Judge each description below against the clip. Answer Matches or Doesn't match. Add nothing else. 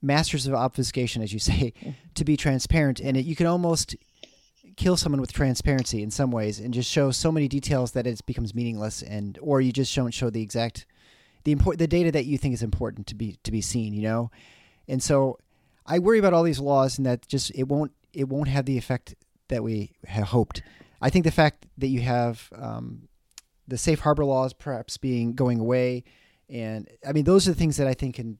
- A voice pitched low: Matches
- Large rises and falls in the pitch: Doesn't match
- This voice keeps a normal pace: Doesn't match